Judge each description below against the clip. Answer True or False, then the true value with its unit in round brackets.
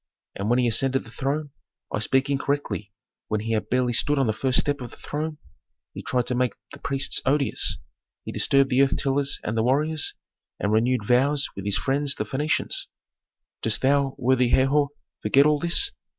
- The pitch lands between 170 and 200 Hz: False (135 Hz)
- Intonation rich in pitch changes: False (2.9 semitones)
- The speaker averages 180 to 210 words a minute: True (190 wpm)